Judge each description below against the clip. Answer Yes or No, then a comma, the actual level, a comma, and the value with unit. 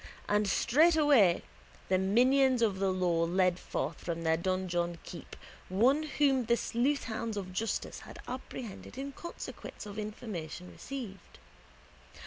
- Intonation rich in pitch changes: Yes, wide, 5.9 semitones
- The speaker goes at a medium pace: No, slow, 125 wpm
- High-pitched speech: Yes, high, 210 Hz